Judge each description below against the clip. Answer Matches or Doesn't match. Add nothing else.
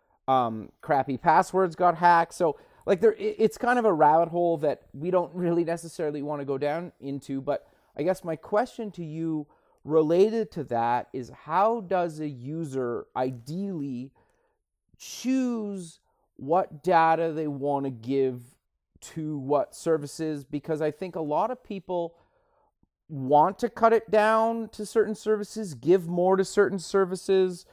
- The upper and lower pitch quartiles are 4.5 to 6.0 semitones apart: Matches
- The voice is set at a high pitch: Doesn't match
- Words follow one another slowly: Doesn't match